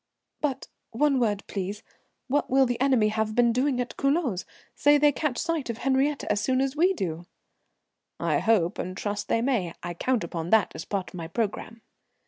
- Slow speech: No, average, 190 wpm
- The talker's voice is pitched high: Yes, high, 235 Hz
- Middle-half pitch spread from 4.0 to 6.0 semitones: Yes, average, 4.9 semitones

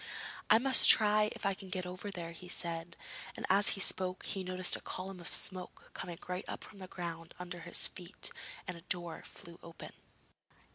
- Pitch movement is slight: Yes, narrow, 2.0 semitones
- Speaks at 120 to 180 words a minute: No, average, 195 wpm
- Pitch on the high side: No, medium, 180 Hz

